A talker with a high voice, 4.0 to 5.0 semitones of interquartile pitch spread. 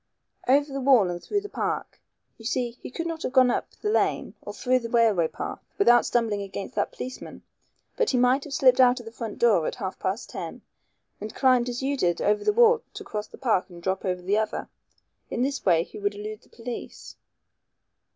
Yes: high, 240 Hz; average, 4.4 semitones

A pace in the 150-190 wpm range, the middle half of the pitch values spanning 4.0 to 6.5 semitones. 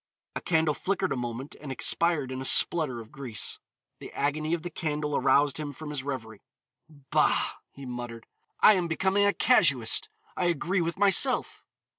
Yes: average, 170 wpm; average, 4.6 semitones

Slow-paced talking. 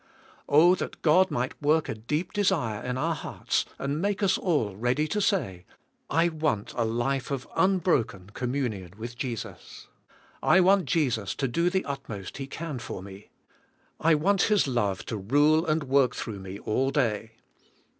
No: average, 175 wpm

